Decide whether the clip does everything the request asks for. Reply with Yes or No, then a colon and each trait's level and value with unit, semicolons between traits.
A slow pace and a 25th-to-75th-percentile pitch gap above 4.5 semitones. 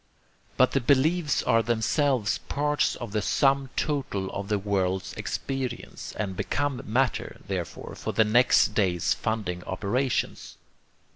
Yes: slow, 130 wpm; average, 5.2 semitones